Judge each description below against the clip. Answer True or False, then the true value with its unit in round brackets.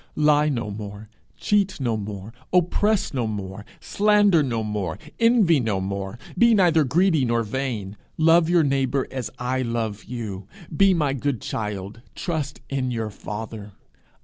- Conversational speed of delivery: True (150 wpm)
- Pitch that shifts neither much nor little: False (7.2 semitones)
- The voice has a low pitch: True (125 Hz)